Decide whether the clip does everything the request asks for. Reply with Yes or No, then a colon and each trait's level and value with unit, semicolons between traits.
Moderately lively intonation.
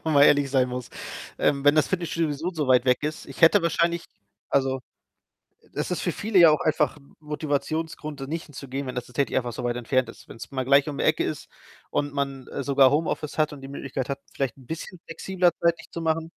Yes: average, 3.2 semitones